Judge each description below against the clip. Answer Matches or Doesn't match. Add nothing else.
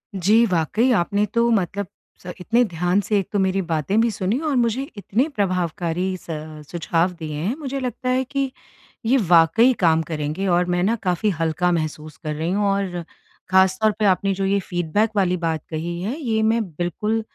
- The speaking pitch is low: Doesn't match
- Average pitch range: Matches